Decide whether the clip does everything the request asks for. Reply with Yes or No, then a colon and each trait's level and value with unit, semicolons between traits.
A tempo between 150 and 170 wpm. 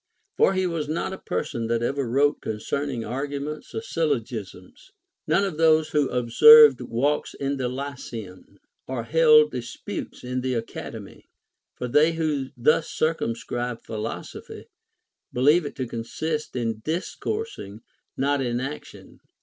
No: slow, 135 wpm